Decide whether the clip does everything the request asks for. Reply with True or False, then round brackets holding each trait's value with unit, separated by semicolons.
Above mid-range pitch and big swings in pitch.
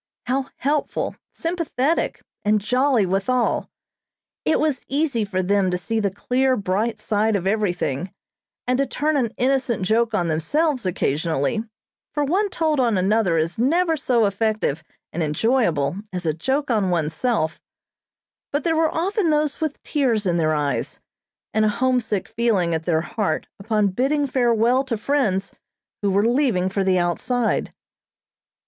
True (225 Hz; 6.4 semitones)